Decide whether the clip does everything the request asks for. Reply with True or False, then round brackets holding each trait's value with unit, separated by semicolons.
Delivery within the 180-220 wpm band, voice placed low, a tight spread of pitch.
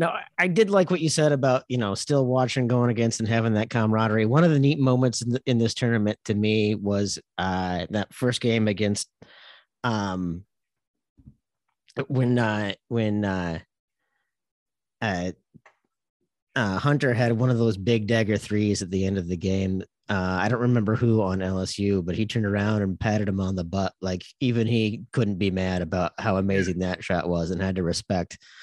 False (185 wpm; 105 Hz; 4.2 semitones)